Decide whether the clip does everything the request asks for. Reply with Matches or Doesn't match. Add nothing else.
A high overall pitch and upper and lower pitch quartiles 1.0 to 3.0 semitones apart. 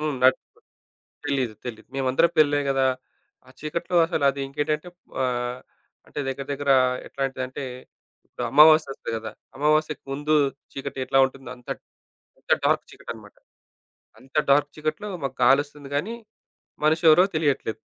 Doesn't match